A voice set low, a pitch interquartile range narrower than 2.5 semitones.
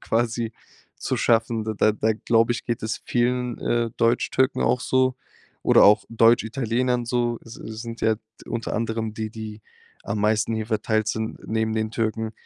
Yes: low, 115 Hz; narrow, 1.3 semitones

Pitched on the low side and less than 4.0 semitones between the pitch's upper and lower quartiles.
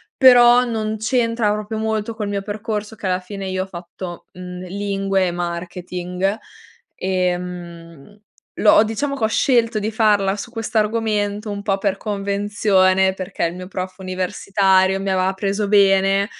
No: high, 200 Hz; narrow, 2.4 semitones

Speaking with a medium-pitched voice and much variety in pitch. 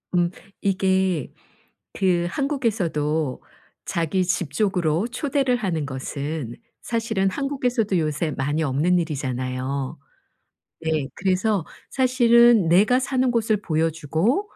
Yes: medium, 180 Hz; wide, 7.0 semitones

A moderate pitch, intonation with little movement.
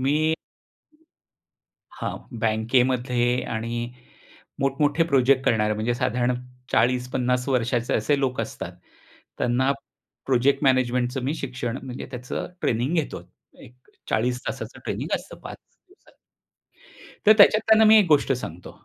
No: low, 125 Hz; narrow, 2.1 semitones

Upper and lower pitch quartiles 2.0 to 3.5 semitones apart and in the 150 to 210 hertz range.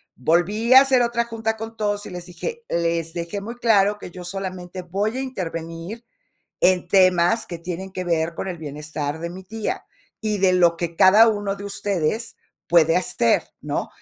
No: average, 4.2 semitones; medium, 185 Hz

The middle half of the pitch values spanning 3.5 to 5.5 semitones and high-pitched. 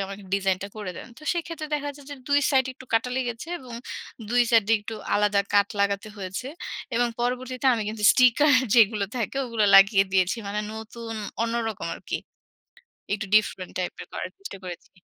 Yes: average, 3.8 semitones; high, 225 Hz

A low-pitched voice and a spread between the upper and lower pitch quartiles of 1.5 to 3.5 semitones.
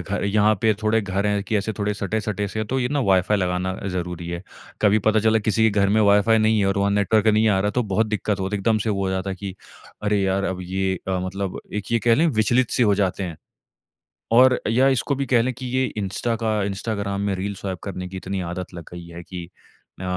Yes: low, 100 Hz; narrow, 2.5 semitones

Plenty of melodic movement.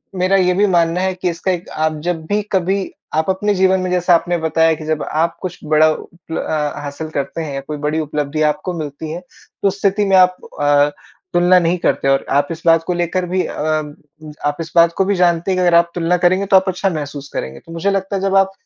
No: average, 3.0 semitones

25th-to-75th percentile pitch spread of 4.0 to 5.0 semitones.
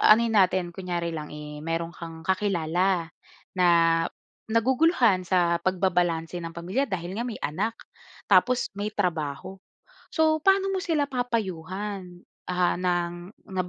Yes: average, 4.7 semitones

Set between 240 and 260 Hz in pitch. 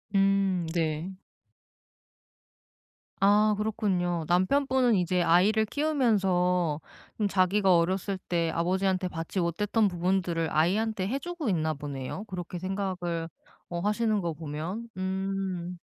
No: medium, 185 Hz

